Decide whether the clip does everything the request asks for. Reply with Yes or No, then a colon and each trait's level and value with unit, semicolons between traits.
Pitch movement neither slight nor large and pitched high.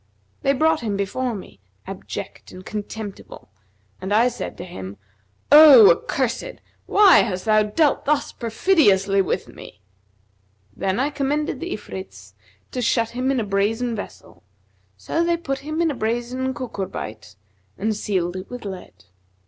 No: wide, 5.8 semitones; high, 230 Hz